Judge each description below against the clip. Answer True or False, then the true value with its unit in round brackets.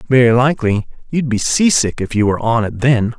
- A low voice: True (120 Hz)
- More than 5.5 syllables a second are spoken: True (5.7 syllables/s)